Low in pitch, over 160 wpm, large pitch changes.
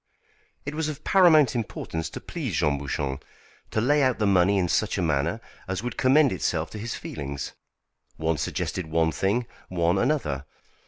Yes: very low, 95 Hz; average, 170 wpm; wide, 7.7 semitones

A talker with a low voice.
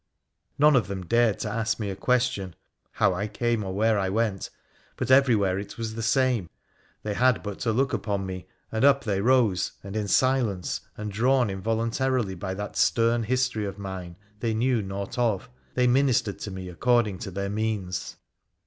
Yes: low, 110 Hz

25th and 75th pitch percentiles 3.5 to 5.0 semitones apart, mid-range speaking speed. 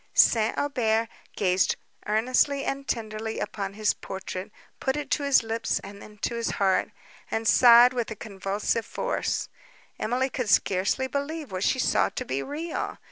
Yes: average, 4.3 semitones; average, 160 wpm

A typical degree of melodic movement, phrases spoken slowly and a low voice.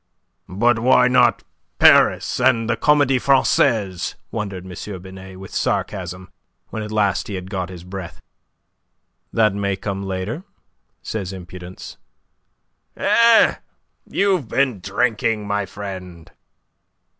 Yes: average, 4.0 semitones; slow, 115 wpm; low, 100 Hz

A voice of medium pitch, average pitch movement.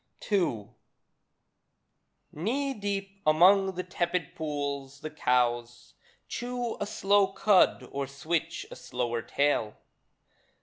No: medium, 165 Hz; wide, 6.1 semitones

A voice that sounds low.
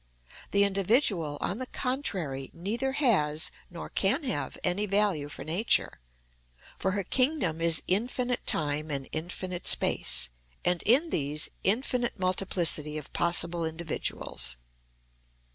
No: medium, 185 Hz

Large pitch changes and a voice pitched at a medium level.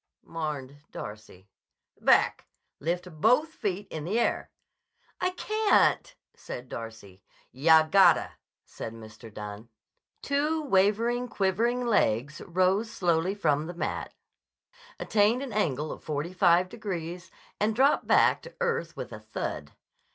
Yes: wide, 7.8 semitones; medium, 180 Hz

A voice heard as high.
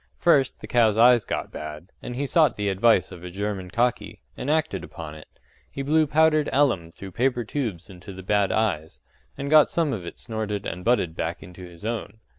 No: low, 110 Hz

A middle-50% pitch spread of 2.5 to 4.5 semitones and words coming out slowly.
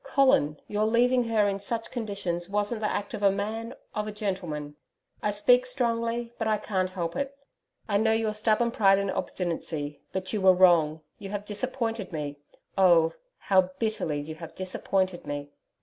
No: average, 3.9 semitones; average, 175 wpm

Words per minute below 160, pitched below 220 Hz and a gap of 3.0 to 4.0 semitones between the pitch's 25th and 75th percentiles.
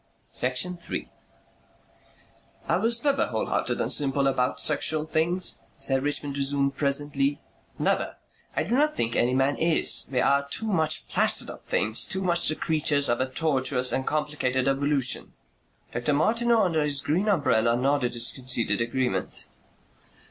Yes: average, 150 wpm; medium, 140 Hz; average, 3.4 semitones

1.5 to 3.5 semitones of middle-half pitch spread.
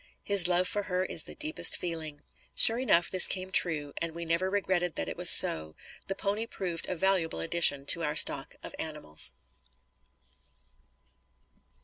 Yes: average, 3.2 semitones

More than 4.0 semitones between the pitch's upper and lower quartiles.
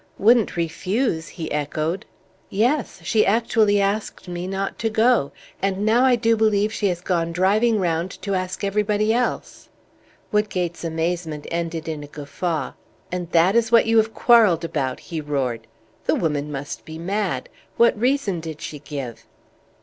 Yes: average, 5.0 semitones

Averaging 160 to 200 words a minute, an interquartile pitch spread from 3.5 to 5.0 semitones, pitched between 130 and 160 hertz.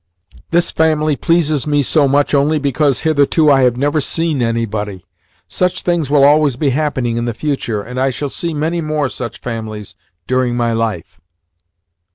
Yes: average, 170 wpm; average, 4.3 semitones; medium, 140 Hz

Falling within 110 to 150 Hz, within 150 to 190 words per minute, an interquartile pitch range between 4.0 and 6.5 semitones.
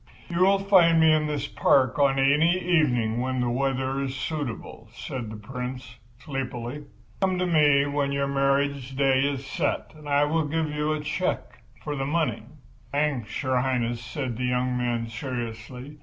No: low, 135 Hz; average, 170 wpm; average, 3.2 semitones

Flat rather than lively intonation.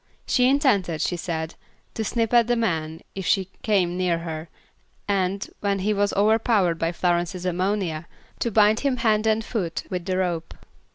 No: average, 4.0 semitones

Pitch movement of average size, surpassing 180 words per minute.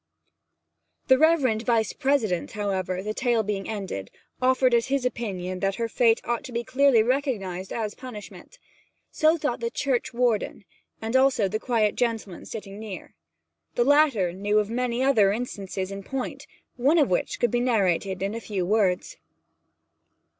No: average, 4.3 semitones; average, 160 wpm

